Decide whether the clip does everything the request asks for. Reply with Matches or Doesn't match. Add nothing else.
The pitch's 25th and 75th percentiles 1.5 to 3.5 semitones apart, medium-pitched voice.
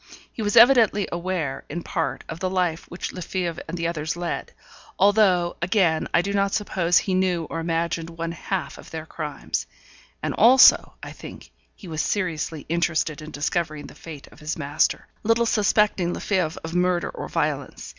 Matches